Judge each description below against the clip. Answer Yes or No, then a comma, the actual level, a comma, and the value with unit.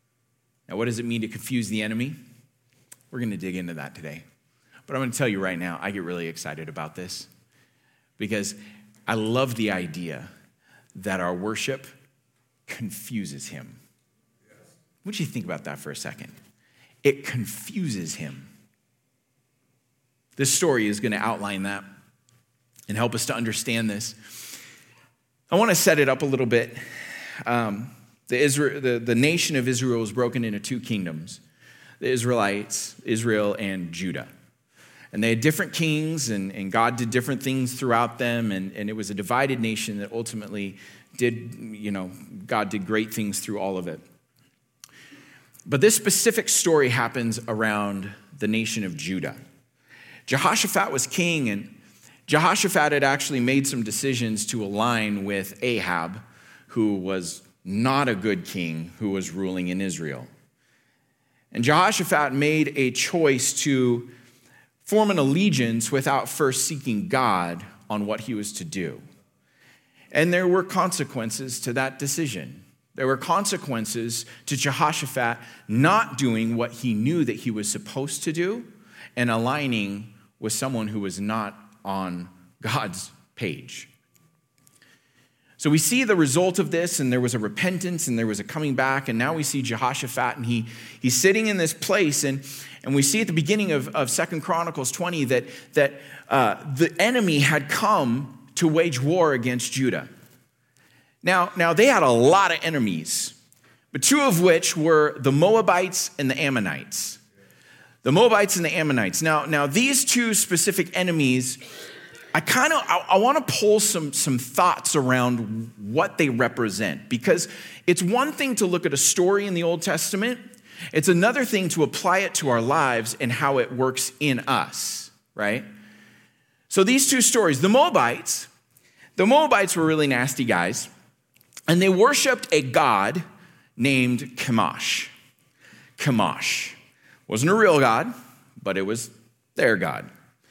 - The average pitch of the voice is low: Yes, low, 130 Hz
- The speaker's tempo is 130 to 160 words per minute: Yes, average, 155 wpm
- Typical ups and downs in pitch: No, wide, 6.1 semitones